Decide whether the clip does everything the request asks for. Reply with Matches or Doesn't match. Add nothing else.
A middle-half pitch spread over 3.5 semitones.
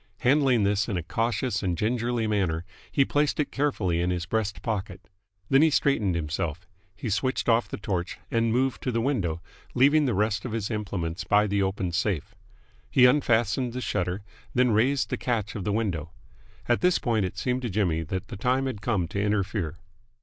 Matches